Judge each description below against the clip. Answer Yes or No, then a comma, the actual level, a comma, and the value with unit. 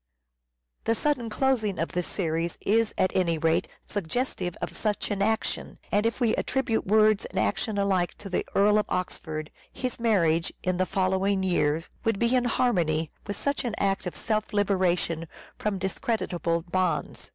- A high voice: Yes, high, 195 Hz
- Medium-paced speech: Yes, average, 165 wpm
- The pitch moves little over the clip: No, average, 4.1 semitones